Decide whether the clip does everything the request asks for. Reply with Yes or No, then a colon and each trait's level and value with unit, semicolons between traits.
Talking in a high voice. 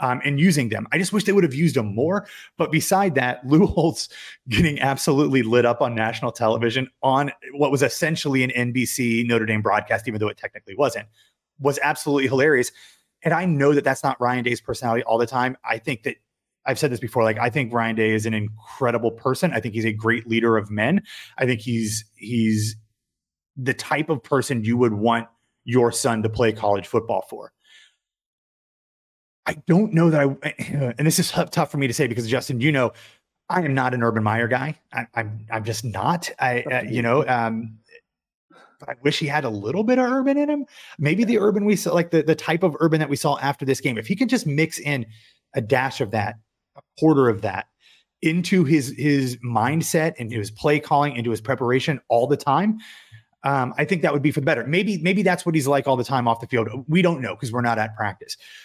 No: low, 135 Hz